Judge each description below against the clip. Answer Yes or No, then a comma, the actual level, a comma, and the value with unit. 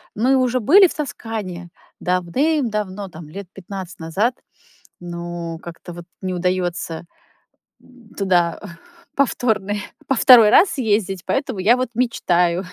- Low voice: No, high, 195 Hz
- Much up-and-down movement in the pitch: Yes, wide, 5.7 semitones